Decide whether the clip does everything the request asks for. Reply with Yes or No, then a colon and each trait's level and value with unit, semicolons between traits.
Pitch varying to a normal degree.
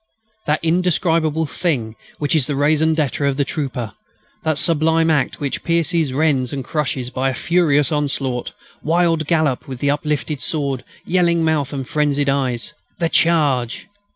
Yes: average, 3.1 semitones